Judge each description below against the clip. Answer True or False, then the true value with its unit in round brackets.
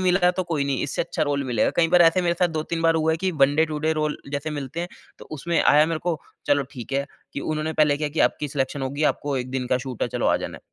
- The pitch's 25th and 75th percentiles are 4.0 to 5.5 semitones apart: False (2.8 semitones)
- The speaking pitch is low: False (150 Hz)